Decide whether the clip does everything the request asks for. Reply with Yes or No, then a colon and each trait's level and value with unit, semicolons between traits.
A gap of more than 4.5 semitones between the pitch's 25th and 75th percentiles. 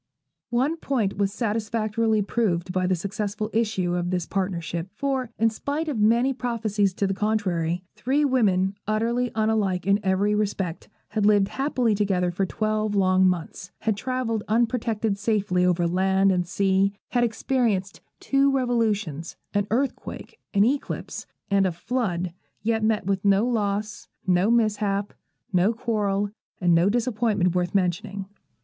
No: average, 3.3 semitones